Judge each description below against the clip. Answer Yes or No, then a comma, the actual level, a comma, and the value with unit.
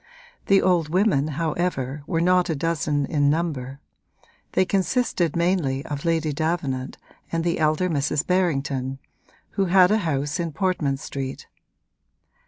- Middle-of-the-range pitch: Yes, medium, 160 Hz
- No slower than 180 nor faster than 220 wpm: No, slow, 135 wpm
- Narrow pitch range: No, average, 4.1 semitones